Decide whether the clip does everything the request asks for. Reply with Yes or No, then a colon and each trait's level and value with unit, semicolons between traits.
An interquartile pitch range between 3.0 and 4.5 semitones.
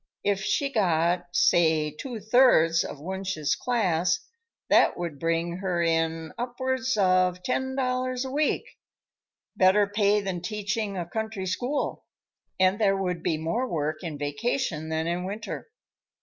No: average, 5.1 semitones